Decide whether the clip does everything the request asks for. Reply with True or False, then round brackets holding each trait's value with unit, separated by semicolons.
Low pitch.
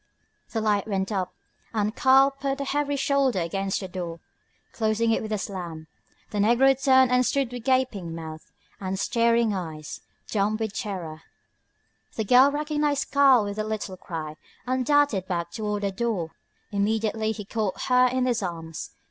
False (215 Hz)